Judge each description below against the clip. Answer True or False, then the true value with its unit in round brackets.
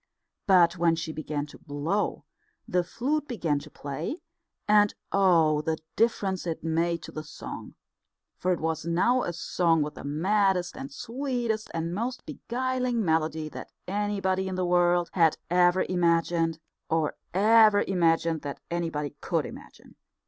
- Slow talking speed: False (150 wpm)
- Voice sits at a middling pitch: True (175 Hz)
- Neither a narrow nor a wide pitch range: True (4.1 semitones)